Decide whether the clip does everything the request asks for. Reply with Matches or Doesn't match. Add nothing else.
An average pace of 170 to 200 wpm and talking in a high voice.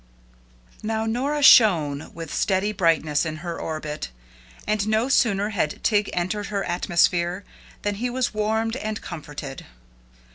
Doesn't match